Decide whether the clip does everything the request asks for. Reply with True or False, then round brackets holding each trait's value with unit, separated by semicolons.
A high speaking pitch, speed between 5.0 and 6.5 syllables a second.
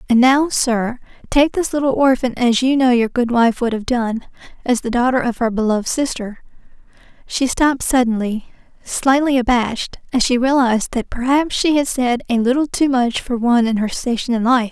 True (245 Hz; 5.2 syllables/s)